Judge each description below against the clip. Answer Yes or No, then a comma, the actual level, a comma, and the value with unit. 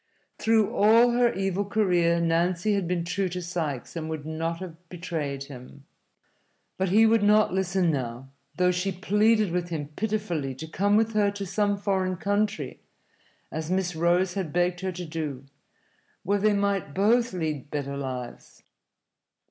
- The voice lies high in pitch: No, medium, 180 Hz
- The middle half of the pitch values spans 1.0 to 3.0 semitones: No, average, 4.0 semitones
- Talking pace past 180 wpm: No, average, 160 wpm